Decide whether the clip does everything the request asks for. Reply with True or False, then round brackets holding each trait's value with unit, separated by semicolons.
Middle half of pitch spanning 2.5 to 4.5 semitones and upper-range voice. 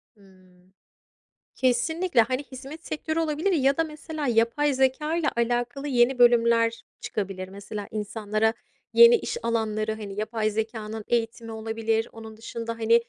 True (3.8 semitones; 230 Hz)